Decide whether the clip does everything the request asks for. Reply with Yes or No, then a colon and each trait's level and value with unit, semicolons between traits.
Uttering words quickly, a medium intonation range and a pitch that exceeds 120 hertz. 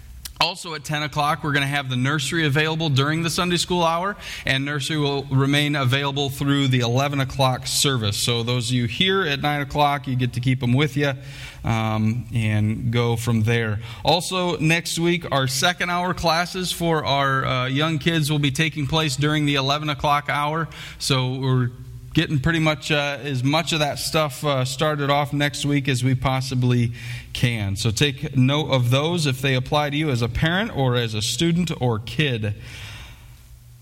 No: average, 190 wpm; average, 3.5 semitones; medium, 140 Hz